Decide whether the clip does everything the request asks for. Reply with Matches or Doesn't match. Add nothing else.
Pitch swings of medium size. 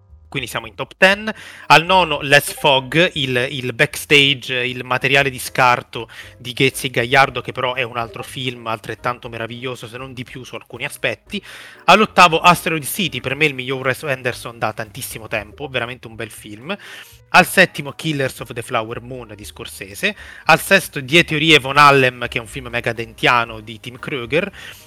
Matches